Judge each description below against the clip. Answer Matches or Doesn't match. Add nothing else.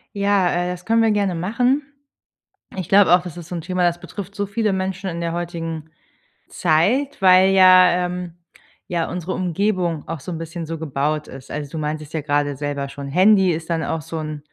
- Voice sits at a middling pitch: Matches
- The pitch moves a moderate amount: Matches